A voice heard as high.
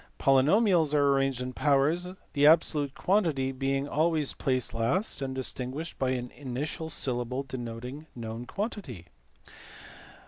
No: low, 135 Hz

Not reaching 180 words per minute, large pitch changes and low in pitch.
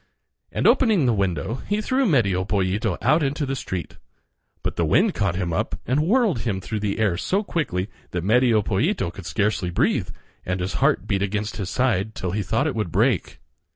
No: average, 195 wpm; wide, 6.5 semitones; low, 105 Hz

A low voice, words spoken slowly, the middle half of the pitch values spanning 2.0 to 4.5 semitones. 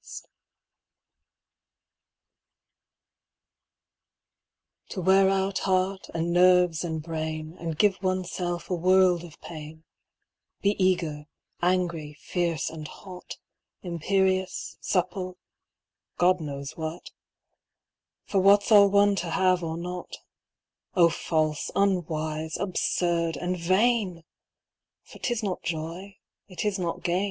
No: medium, 180 Hz; slow, 110 wpm; narrow, 2.5 semitones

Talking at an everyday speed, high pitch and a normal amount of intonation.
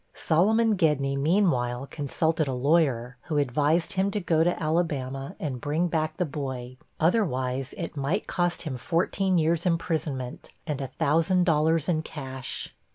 No: average, 150 wpm; medium, 155 Hz; average, 4.1 semitones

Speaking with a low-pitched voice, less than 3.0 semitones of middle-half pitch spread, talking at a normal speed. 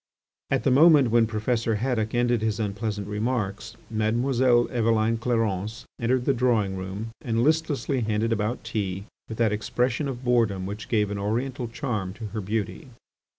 Yes: low, 115 Hz; narrow, 2.6 semitones; average, 155 wpm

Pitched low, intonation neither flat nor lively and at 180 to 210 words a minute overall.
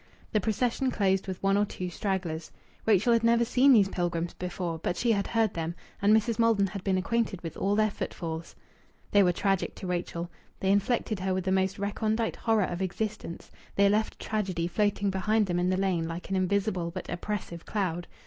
No: high, 195 Hz; average, 3.2 semitones; average, 195 wpm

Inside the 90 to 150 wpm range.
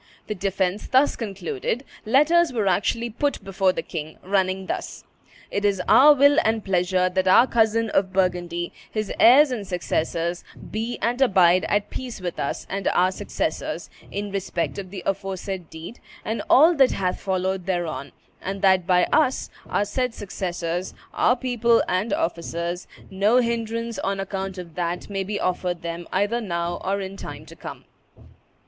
No: average, 165 wpm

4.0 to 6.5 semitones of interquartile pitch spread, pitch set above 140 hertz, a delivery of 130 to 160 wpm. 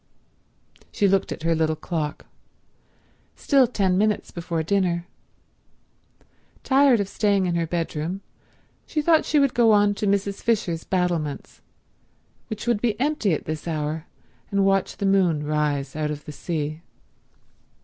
Yes: average, 4.7 semitones; medium, 185 Hz; average, 145 wpm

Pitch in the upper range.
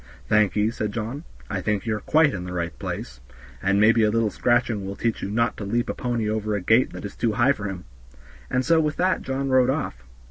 No: low, 110 Hz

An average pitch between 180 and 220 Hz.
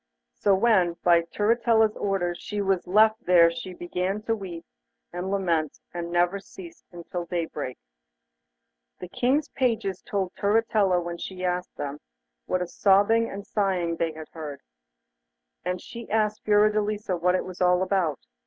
Yes: medium, 185 Hz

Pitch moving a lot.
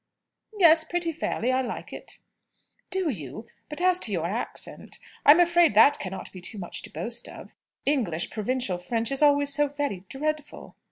Yes: wide, 6.8 semitones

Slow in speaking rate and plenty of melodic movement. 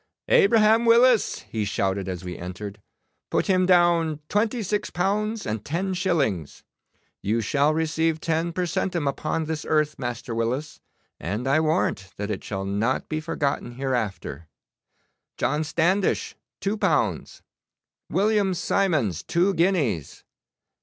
Yes: slow, 130 wpm; wide, 8.7 semitones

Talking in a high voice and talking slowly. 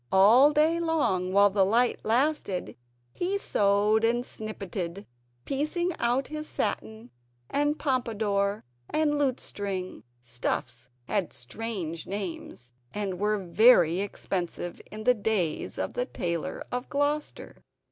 Yes: high, 215 Hz; slow, 115 wpm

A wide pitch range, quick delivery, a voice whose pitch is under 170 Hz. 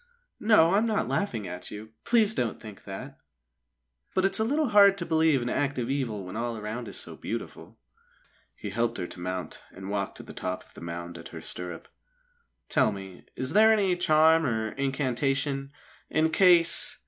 No: wide, 8.8 semitones; average, 185 wpm; low, 135 Hz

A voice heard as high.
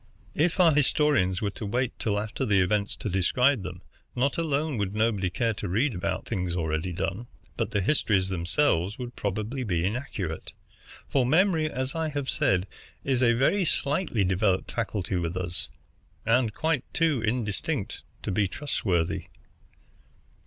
No: low, 110 Hz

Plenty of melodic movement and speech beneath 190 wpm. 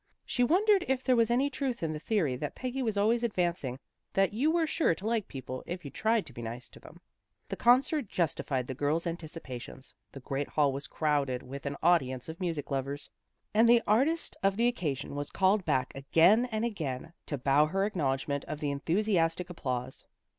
No: wide, 8.2 semitones; average, 195 wpm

